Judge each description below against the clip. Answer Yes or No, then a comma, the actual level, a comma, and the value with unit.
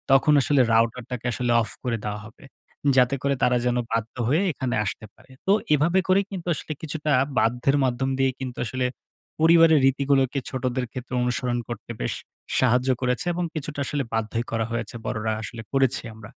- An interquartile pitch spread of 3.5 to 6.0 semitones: No, average, 3.1 semitones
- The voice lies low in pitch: Yes, low, 125 Hz